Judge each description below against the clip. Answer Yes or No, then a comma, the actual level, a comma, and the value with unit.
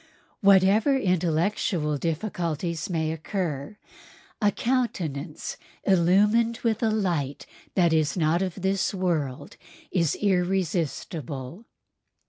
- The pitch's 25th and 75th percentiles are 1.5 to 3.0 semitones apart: No, average, 4.1 semitones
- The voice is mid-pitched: Yes, medium, 180 Hz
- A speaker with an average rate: No, slow, 95 wpm